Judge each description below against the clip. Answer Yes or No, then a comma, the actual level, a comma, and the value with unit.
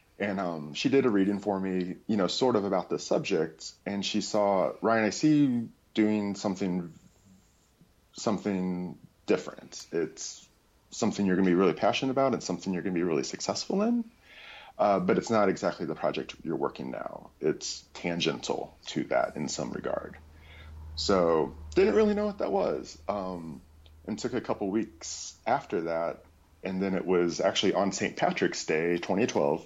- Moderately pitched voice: No, very low, 95 Hz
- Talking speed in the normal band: Yes, average, 175 wpm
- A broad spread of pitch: No, average, 3.6 semitones